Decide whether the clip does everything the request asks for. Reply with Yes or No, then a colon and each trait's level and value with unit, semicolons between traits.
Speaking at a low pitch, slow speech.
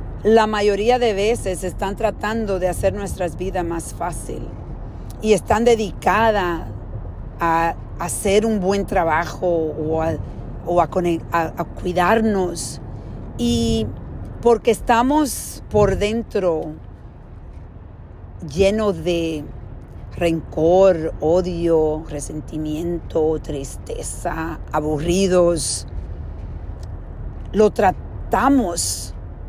No: medium, 165 Hz; slow, 90 wpm